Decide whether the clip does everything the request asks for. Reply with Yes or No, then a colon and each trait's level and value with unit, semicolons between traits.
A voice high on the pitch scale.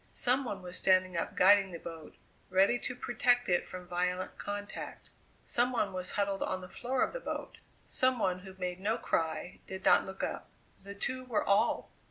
Yes: high, 195 Hz